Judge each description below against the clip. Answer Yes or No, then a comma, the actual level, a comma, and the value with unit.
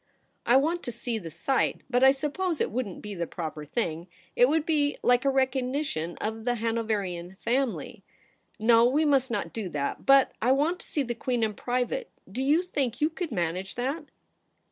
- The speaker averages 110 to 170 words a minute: No, average, 195 wpm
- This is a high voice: Yes, high, 245 Hz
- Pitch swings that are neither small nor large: Yes, average, 4.5 semitones